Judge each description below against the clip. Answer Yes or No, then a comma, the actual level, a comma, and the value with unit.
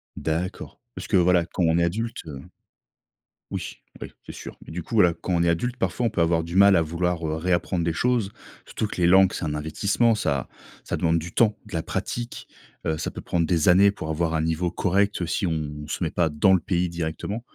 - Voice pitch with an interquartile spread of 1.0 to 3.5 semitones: Yes, average, 3.0 semitones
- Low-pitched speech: Yes, very low, 85 Hz